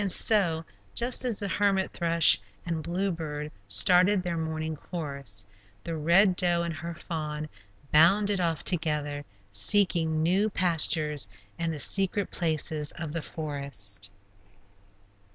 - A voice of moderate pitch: Yes, medium, 165 Hz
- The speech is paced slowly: Yes, slow, 125 wpm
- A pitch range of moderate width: Yes, average, 3.3 semitones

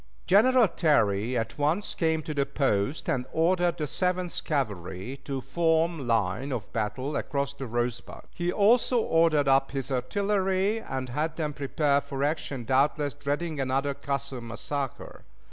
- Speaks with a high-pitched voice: No, medium, 140 Hz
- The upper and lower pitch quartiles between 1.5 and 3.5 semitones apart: No, average, 4.1 semitones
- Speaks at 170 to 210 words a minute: No, average, 145 wpm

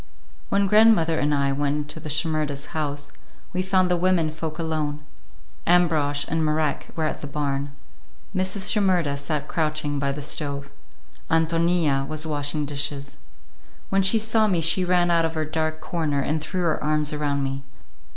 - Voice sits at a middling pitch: Yes, medium, 155 Hz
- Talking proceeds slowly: No, average, 165 wpm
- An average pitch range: Yes, average, 3.0 semitones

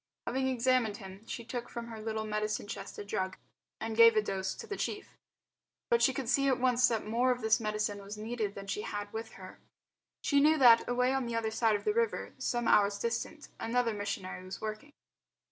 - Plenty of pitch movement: No, average, 3.0 semitones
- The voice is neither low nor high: No, high, 225 Hz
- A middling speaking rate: No, fast, 215 wpm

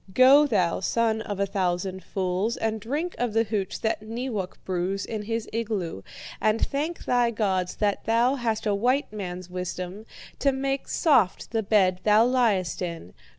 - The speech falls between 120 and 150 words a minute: No, average, 165 wpm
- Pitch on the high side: Yes, high, 215 Hz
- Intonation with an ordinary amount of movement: Yes, average, 4.0 semitones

